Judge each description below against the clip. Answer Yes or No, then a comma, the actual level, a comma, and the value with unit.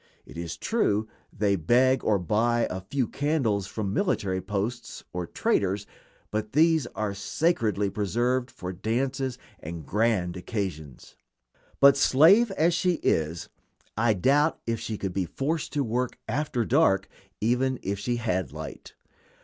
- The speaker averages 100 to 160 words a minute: Yes, average, 140 wpm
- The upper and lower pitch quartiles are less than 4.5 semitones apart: No, wide, 5.5 semitones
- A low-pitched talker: Yes, low, 110 Hz